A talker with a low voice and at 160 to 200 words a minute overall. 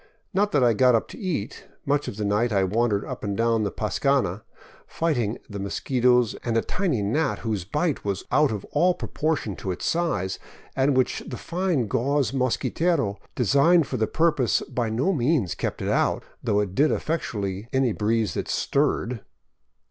Yes: low, 120 Hz; average, 175 wpm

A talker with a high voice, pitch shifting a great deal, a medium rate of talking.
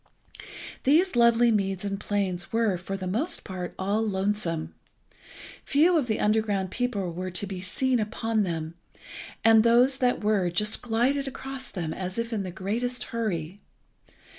No: high, 210 Hz; average, 4.2 semitones; average, 155 wpm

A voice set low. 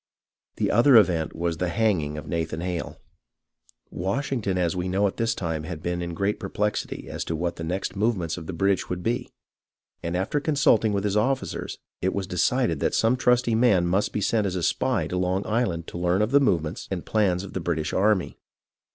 Yes: very low, 95 Hz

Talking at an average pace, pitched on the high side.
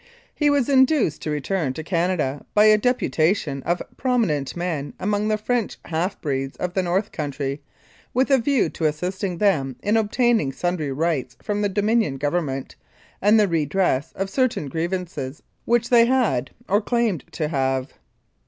No: average, 160 wpm; medium, 180 Hz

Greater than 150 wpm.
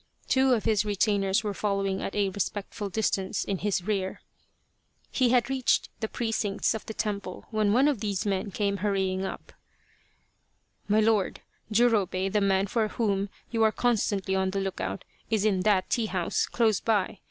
Yes: average, 175 wpm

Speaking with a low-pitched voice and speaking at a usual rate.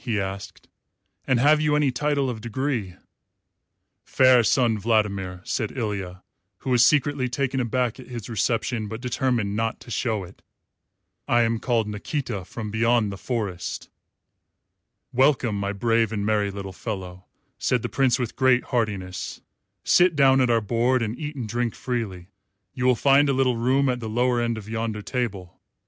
Yes: low, 115 Hz; average, 165 wpm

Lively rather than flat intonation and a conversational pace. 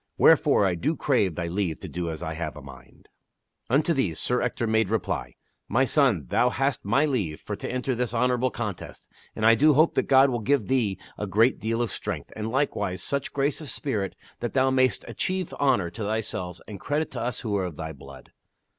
No: wide, 5.9 semitones; fast, 215 wpm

